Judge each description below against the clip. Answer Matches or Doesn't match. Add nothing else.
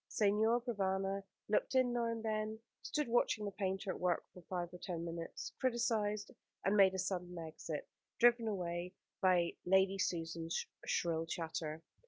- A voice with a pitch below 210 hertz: Matches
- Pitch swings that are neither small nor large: Matches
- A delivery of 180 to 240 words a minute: Doesn't match